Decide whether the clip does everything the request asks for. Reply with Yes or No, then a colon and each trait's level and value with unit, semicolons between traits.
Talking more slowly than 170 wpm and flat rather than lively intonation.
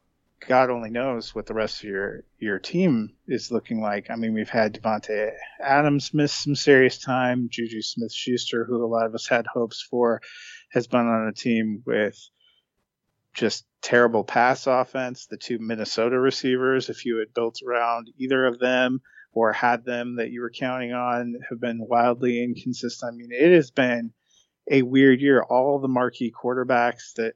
No: average, 180 wpm; narrow, 2.0 semitones